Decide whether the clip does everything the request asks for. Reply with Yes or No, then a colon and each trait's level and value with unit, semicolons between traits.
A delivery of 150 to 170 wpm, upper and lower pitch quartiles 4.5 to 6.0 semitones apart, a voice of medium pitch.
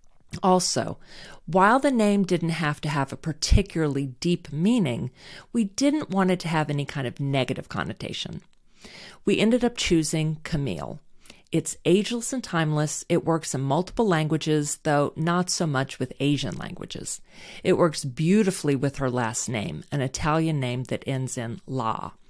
Yes: average, 155 wpm; average, 4.8 semitones; medium, 160 Hz